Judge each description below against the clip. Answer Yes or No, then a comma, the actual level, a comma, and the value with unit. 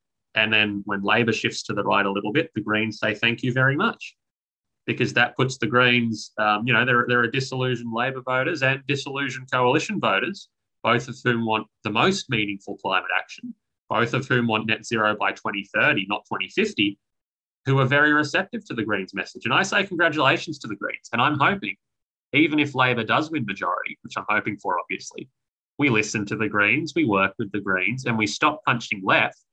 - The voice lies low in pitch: Yes, low, 120 Hz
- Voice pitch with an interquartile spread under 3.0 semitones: No, average, 3.9 semitones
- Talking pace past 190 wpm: Yes, average, 200 wpm